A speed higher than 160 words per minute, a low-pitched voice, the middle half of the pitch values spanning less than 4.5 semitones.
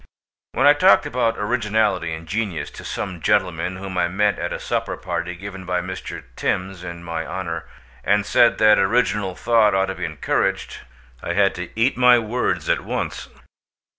Yes: average, 175 wpm; very low, 95 Hz; average, 3.3 semitones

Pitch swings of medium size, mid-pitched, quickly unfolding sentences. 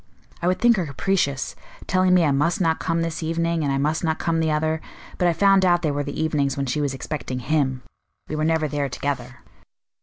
Yes: average, 3.1 semitones; medium, 155 Hz; fast, 225 wpm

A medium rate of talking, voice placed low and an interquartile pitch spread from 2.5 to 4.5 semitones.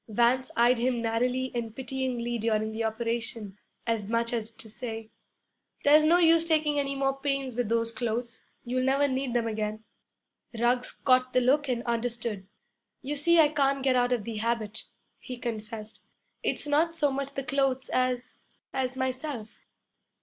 No: average, 165 wpm; high, 245 Hz; average, 2.9 semitones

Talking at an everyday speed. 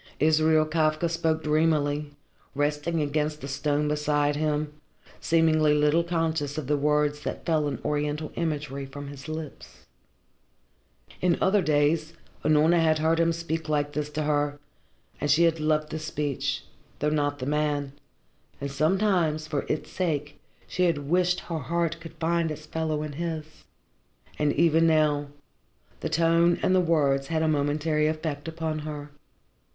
Yes: average, 155 wpm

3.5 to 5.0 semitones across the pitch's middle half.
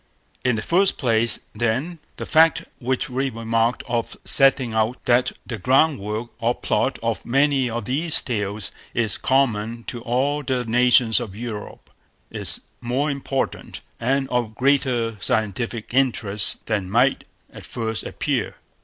No: average, 3.1 semitones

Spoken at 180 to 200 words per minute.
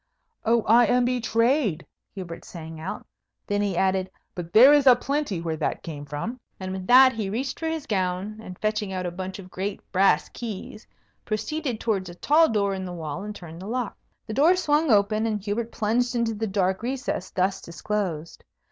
Yes: average, 195 wpm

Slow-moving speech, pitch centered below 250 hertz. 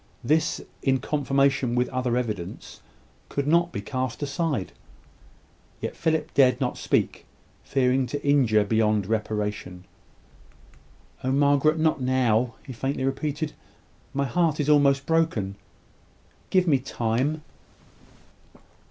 Yes: slow, 115 wpm; low, 135 Hz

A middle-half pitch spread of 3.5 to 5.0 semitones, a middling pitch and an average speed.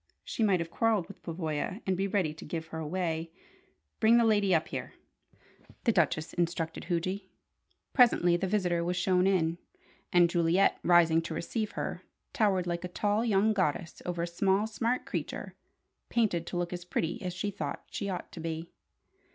No: average, 3.0 semitones; medium, 180 Hz; average, 175 wpm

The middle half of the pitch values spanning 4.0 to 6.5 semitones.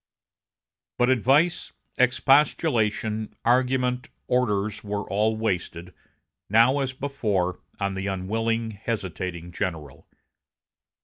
Yes: average, 4.6 semitones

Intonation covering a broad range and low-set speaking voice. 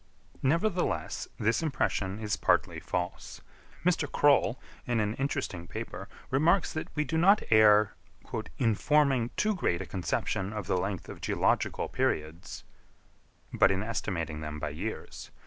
Yes: wide, 8.0 semitones; low, 110 Hz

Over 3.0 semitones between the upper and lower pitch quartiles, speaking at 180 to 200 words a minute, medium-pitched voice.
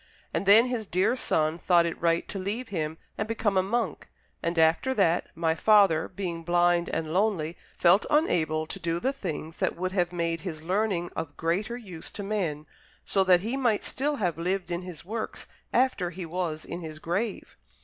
Yes: average, 3.8 semitones; average, 190 wpm; medium, 180 Hz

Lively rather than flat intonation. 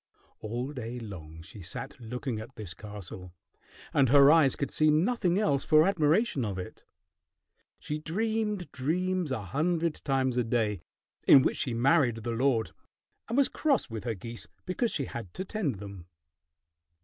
Yes: wide, 6.8 semitones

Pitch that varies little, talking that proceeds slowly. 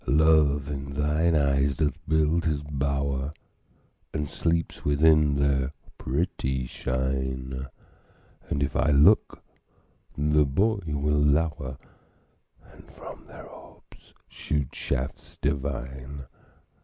Yes: narrow, 1.9 semitones; slow, 105 wpm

